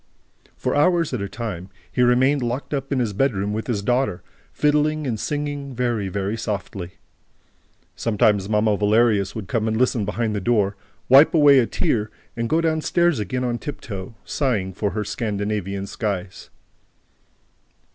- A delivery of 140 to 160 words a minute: Yes, average, 155 wpm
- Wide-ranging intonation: No, average, 4.6 semitones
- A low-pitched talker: Yes, low, 115 Hz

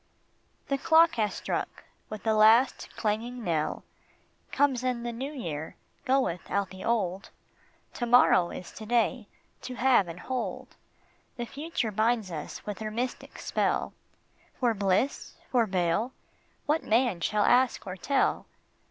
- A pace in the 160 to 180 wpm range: No, average, 145 wpm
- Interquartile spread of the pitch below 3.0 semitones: No, average, 4.5 semitones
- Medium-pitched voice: No, high, 230 Hz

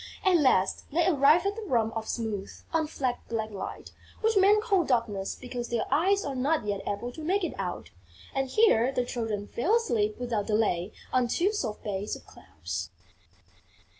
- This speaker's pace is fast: No, average, 175 wpm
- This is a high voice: Yes, very high, 250 Hz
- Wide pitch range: Yes, wide, 7.7 semitones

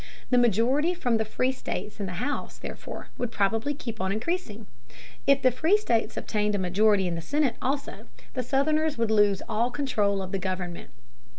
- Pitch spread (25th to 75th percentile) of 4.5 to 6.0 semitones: Yes, wide, 5.4 semitones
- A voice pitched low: No, high, 225 Hz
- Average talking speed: Yes, average, 185 wpm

